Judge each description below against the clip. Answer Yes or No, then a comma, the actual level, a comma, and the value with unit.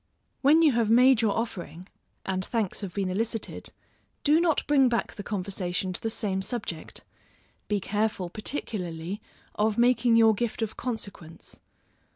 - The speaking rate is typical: Yes, average, 150 wpm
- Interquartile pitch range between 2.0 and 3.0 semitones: No, average, 3.8 semitones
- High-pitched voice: Yes, high, 215 Hz